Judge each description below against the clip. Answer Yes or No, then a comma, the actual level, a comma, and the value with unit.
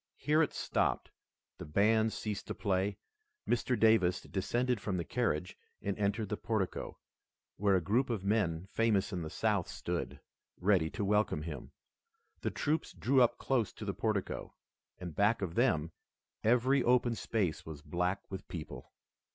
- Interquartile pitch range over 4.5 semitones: No, average, 4.1 semitones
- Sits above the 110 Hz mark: No, low, 105 Hz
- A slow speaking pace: No, average, 160 wpm